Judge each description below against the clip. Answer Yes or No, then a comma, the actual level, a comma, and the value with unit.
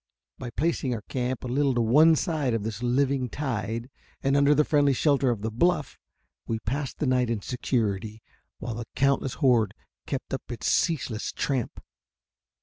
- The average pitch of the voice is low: Yes, low, 125 Hz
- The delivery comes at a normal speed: Yes, average, 170 wpm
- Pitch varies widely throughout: No, average, 3.5 semitones